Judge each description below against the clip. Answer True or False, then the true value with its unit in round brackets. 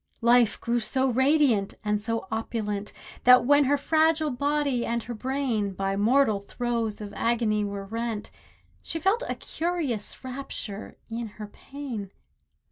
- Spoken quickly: False (140 wpm)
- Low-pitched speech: False (235 Hz)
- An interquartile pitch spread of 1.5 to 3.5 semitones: False (4.7 semitones)